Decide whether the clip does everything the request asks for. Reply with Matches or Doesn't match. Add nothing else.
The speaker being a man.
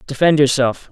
Matches